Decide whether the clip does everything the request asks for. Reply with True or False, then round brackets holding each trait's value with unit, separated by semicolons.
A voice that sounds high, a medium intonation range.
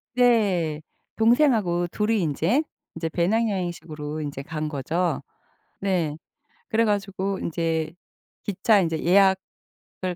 False (180 Hz; 4.3 semitones)